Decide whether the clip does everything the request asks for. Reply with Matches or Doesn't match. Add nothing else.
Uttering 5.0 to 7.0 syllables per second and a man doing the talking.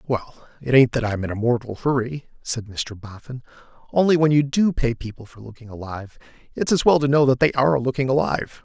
Matches